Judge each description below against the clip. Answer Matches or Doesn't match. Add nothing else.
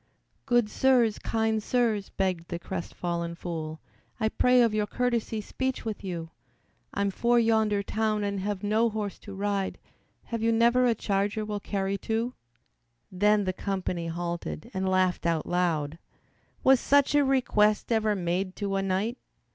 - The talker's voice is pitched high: Matches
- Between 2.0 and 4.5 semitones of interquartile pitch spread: Matches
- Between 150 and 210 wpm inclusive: Matches